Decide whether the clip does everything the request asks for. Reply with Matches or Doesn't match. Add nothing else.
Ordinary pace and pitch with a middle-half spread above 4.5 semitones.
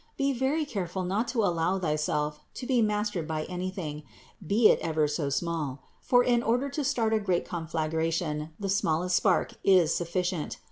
Matches